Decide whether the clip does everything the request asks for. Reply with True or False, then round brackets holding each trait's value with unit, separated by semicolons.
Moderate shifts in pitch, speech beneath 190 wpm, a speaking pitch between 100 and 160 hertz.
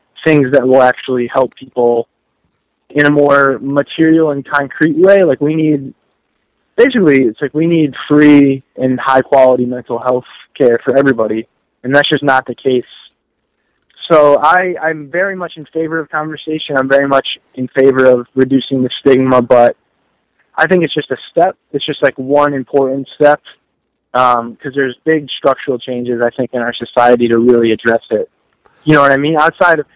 True (3.1 semitones; 180 wpm; 140 Hz)